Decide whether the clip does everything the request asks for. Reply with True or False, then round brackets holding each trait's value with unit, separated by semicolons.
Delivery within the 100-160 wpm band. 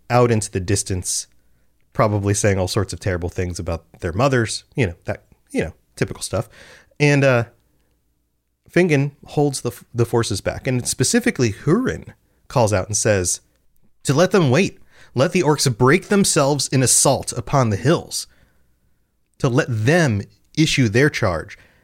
True (155 wpm)